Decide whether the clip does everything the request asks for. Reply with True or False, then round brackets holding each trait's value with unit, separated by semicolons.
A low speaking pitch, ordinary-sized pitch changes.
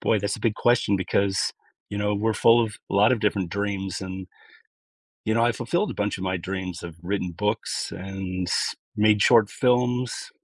True (100 Hz; 3.1 semitones)